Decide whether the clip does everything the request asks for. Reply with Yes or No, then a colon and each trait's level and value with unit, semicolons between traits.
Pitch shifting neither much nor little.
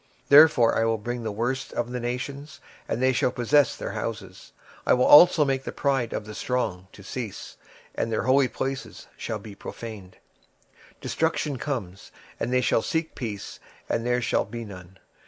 Yes: average, 3.5 semitones